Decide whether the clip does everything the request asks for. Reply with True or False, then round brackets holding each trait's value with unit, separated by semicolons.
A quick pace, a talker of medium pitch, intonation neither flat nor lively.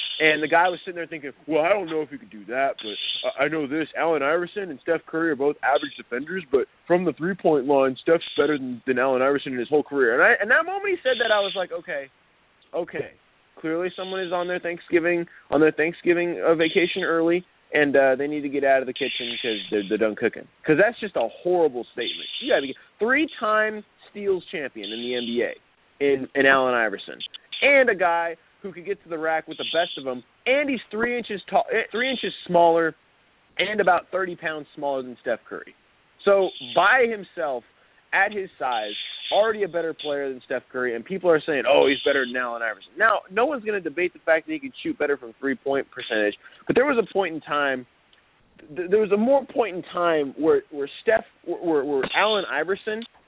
False (215 wpm; 165 Hz; 5.8 semitones)